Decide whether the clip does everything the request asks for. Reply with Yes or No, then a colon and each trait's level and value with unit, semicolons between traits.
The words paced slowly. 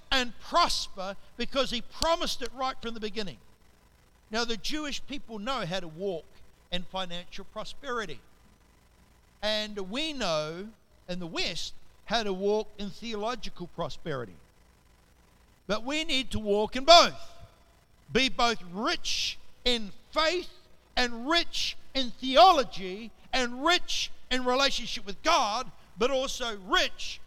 Yes: slow, 130 wpm